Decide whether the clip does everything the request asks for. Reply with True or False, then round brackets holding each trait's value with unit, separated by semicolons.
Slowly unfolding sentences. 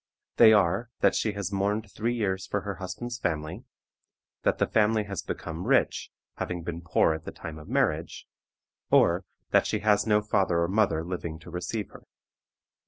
False (175 wpm)